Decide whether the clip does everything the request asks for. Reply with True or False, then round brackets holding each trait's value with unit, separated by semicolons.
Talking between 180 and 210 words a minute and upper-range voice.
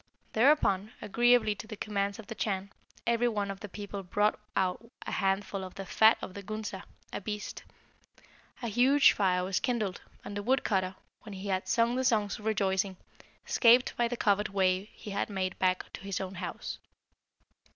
True (185 wpm; 205 Hz)